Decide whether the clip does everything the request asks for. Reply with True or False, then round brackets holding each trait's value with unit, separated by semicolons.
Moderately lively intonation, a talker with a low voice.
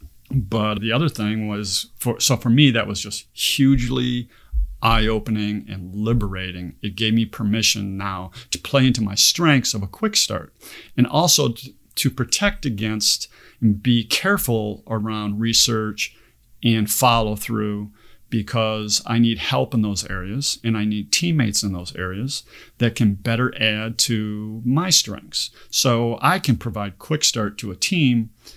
True (3.2 semitones; 110 Hz)